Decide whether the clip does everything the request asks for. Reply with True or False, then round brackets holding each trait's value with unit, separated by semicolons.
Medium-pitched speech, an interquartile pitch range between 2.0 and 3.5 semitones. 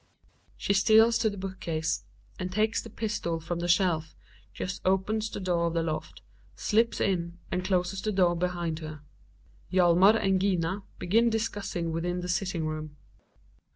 True (180 Hz; 3.1 semitones)